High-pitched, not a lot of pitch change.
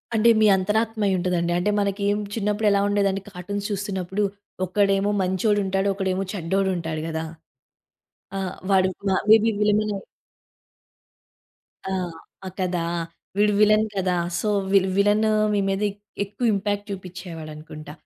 Yes: high, 195 Hz; narrow, 2.1 semitones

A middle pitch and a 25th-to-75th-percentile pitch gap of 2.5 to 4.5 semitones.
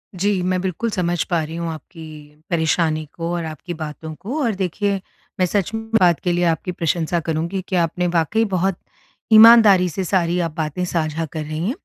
Yes: medium, 175 Hz; average, 2.9 semitones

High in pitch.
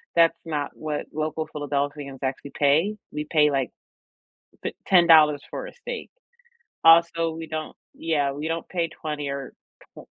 No: medium, 155 Hz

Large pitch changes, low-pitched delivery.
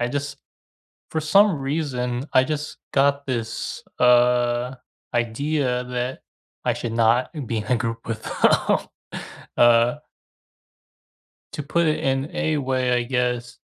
No: average, 2.9 semitones; low, 125 Hz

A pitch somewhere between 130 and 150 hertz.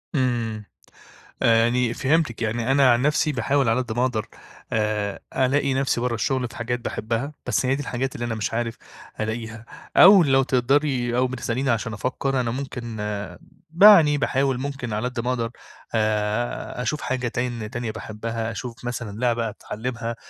No: low, 120 Hz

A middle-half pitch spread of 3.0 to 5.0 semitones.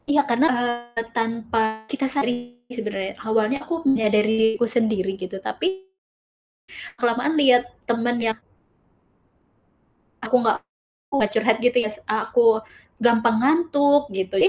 No: narrow, 2.4 semitones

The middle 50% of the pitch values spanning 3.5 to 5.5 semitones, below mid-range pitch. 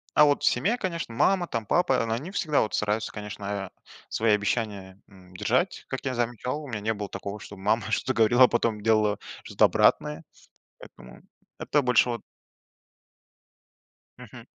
Yes: average, 3.9 semitones; low, 110 Hz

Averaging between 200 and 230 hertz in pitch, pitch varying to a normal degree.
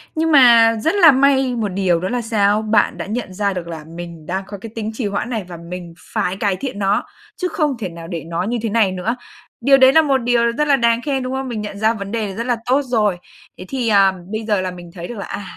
Yes: high, 215 Hz; average, 4.7 semitones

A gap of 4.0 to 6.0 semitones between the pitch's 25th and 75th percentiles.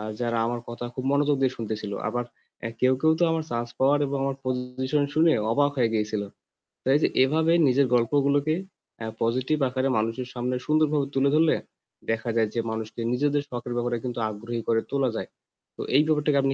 No: average, 3.4 semitones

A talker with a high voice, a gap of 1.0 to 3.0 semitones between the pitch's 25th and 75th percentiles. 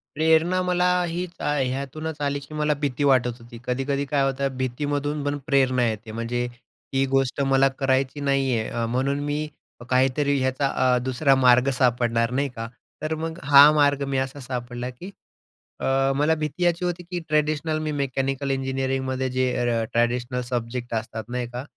No: low, 135 Hz; narrow, 2.6 semitones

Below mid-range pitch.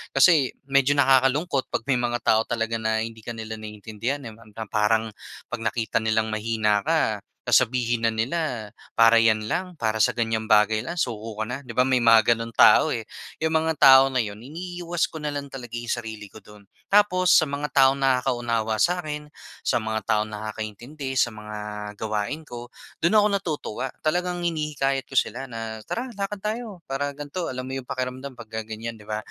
Yes: low, 120 Hz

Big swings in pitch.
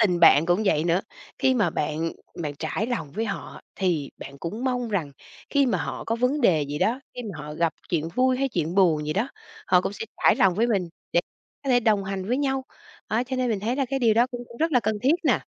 Yes: wide, 6.7 semitones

